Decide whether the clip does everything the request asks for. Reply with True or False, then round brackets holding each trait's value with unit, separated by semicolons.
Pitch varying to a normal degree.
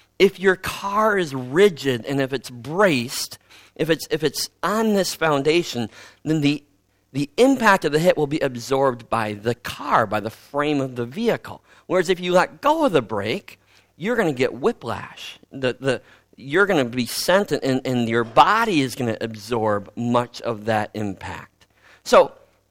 False (7.4 semitones)